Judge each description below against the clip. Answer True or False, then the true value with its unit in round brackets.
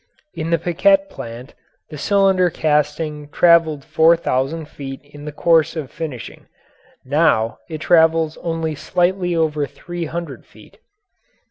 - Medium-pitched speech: True (160 Hz)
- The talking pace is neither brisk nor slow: False (130 wpm)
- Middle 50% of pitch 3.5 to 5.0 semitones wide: False (2.4 semitones)